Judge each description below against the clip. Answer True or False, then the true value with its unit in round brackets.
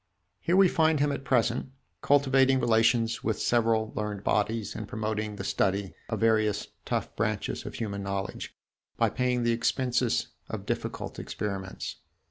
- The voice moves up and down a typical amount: True (3.1 semitones)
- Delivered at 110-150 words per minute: True (145 wpm)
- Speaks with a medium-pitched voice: False (115 Hz)